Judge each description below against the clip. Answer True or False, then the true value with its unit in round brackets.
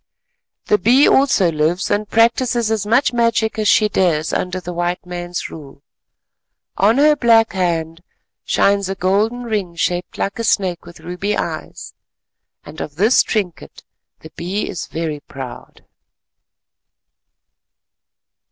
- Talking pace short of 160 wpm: True (135 wpm)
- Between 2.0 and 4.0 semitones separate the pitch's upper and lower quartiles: False (4.7 semitones)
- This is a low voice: False (190 Hz)